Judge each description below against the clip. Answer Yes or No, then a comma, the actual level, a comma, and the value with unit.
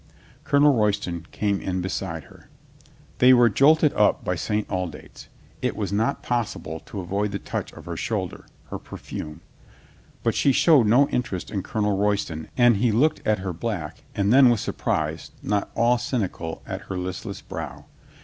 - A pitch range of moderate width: Yes, average, 4.6 semitones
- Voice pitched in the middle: No, low, 105 Hz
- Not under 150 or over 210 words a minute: Yes, average, 170 wpm